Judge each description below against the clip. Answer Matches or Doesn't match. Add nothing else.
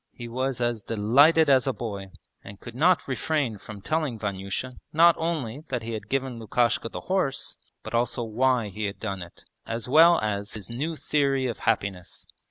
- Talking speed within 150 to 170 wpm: Doesn't match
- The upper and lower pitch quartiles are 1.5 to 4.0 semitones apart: Doesn't match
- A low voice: Matches